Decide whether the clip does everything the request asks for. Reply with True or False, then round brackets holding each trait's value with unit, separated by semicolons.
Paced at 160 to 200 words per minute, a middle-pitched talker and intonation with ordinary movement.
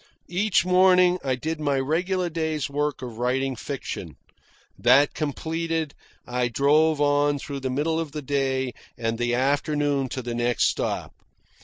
False (150 wpm; 145 Hz; 3.4 semitones)